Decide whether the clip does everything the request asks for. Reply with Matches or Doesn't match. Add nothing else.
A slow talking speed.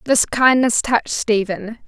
Matches